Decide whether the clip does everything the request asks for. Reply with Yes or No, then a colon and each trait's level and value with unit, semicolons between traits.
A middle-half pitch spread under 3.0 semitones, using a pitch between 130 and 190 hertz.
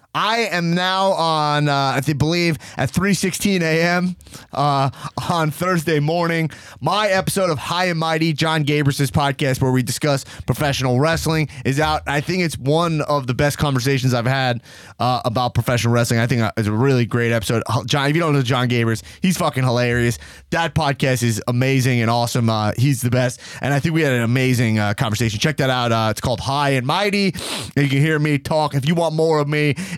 No: average, 4.4 semitones; medium, 140 Hz